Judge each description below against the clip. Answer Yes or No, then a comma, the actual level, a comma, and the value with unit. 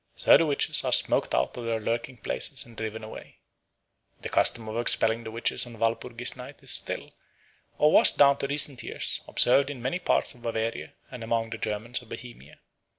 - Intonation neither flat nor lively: No, narrow, 2.1 semitones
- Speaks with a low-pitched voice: Yes, low, 115 Hz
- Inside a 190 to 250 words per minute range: Yes, average, 195 wpm